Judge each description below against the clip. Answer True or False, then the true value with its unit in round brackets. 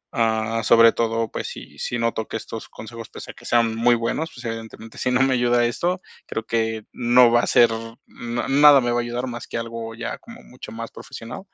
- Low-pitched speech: True (115 Hz)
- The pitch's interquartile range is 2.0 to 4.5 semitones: False (1.2 semitones)